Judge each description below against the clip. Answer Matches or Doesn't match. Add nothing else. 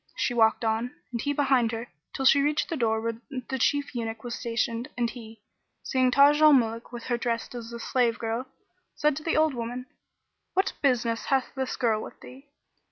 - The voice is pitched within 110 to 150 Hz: Doesn't match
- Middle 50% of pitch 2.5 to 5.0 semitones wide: Matches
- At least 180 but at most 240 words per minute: Matches